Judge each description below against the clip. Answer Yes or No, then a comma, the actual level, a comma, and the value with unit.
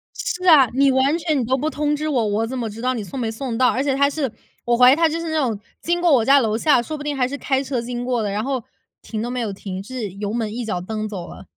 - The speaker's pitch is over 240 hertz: Yes, very high, 255 Hz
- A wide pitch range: No, average, 4.1 semitones